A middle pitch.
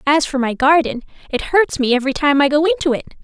No: very high, 290 Hz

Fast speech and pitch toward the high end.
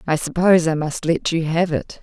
No: fast, 235 wpm; medium, 165 Hz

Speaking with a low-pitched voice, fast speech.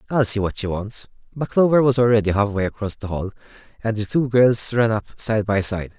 Yes: low, 110 Hz; fast, 220 wpm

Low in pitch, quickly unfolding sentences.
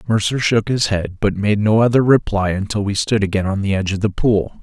Yes: low, 105 Hz; fast, 245 wpm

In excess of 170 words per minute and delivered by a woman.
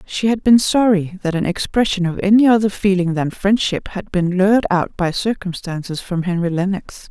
Yes: average, 185 wpm; female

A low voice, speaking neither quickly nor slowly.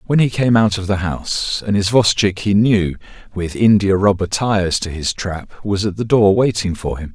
No: low, 100 Hz; fast, 210 wpm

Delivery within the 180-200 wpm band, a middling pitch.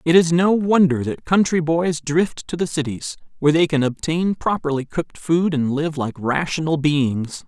Yes: average, 185 wpm; medium, 155 Hz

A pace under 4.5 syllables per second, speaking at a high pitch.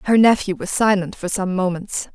No: 5.1 syllables/s; high, 195 Hz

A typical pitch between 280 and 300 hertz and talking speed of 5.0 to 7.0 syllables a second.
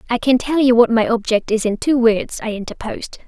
No: high, 235 Hz; 5.7 syllables/s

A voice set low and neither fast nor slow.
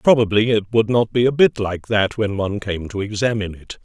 No: low, 110 Hz; fast, 235 wpm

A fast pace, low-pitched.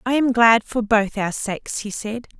No: fast, 225 wpm; high, 225 Hz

